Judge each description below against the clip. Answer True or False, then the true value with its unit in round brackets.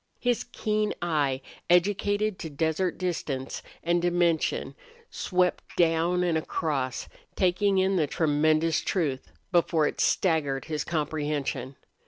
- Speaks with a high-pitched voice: False (165 Hz)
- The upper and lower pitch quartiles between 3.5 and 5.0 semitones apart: False (3.1 semitones)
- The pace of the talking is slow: True (115 wpm)